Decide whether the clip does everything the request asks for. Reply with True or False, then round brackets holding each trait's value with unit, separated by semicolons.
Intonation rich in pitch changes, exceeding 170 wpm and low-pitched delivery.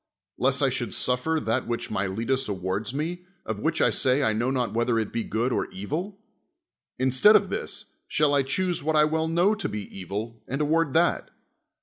True (6.3 semitones; 195 wpm; 130 Hz)